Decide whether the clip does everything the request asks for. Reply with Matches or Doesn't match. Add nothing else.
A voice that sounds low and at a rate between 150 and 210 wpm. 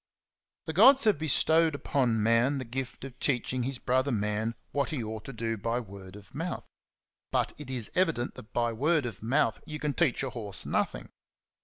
Matches